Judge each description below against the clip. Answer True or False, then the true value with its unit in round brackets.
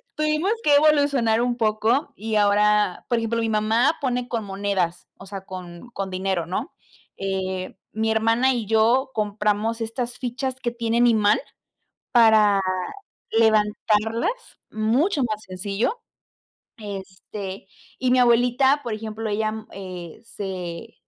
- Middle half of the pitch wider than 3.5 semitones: False (3.2 semitones)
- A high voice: True (220 Hz)